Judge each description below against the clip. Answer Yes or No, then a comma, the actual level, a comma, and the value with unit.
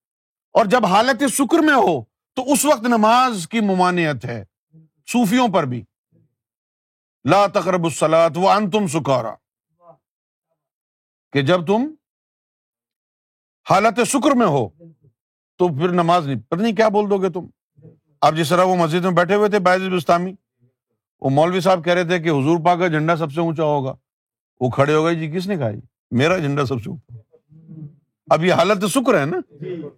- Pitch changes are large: Yes, wide, 5.7 semitones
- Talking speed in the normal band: Yes, average, 165 wpm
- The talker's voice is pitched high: No, medium, 170 Hz